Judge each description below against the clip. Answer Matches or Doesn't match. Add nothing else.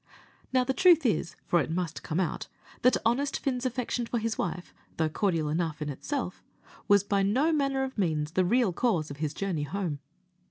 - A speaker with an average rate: Matches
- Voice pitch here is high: Matches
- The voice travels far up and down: Matches